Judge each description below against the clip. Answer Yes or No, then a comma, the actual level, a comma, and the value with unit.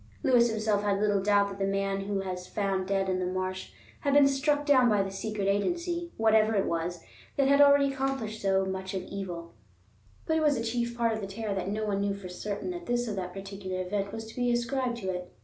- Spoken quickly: Yes, fast, 235 wpm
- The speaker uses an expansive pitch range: No, average, 3.8 semitones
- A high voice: Yes, high, 205 Hz